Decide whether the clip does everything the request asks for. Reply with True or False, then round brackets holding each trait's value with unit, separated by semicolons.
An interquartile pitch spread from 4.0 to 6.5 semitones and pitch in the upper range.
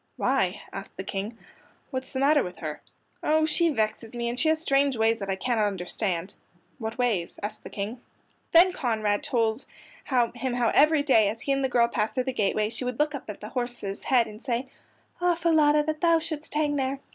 True (5.1 semitones; 245 Hz)